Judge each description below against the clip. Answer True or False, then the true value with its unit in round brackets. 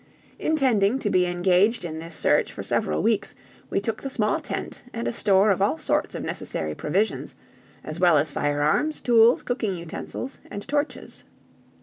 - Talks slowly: False (165 wpm)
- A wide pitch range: True (5.8 semitones)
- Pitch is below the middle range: False (195 Hz)